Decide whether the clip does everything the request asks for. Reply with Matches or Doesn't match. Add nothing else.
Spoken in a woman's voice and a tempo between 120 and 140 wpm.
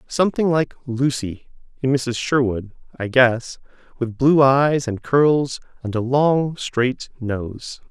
Doesn't match